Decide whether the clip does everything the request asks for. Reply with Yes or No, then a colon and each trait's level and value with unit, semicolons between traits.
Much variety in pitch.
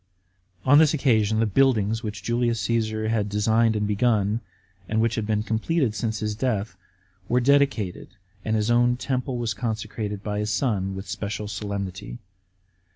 No: narrow, 2.4 semitones